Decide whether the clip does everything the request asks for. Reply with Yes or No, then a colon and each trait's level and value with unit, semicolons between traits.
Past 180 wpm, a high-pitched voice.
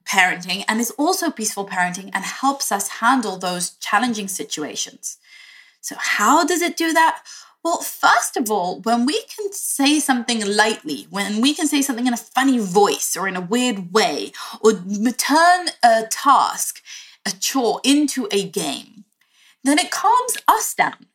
No: average, 160 wpm; high, 240 Hz